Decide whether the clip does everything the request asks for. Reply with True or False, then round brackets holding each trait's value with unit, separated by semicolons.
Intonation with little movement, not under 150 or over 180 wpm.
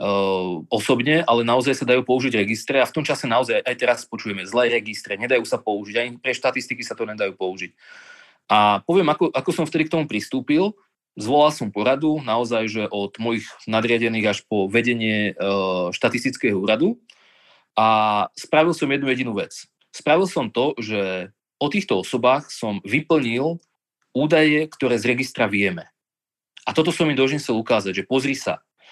False (5.5 semitones; 165 wpm)